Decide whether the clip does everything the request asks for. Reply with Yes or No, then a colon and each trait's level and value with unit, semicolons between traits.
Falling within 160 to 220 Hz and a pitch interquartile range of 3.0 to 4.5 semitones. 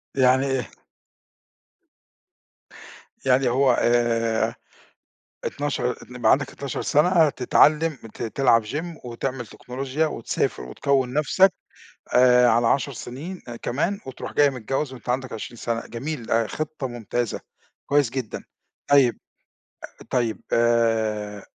No: low, 130 Hz; average, 3.3 semitones